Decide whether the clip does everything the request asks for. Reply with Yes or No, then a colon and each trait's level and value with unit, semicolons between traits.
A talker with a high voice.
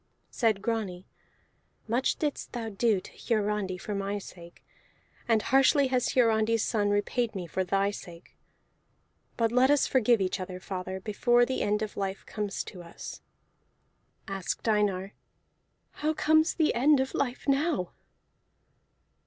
Yes: high, 215 Hz